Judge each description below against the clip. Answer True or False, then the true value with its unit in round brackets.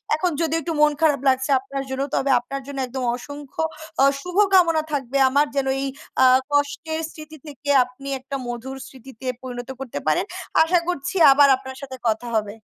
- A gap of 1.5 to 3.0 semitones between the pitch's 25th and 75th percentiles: True (2.7 semitones)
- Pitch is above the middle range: True (275 Hz)